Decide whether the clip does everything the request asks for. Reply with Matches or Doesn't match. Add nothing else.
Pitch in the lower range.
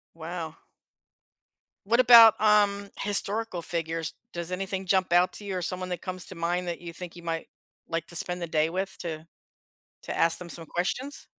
Doesn't match